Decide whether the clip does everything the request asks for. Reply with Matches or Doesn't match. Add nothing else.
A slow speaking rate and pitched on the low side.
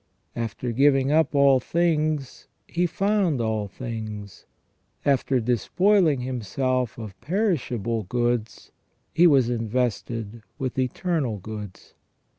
Matches